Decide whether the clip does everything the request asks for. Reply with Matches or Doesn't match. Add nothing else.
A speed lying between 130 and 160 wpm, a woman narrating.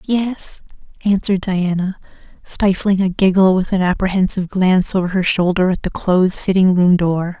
Matches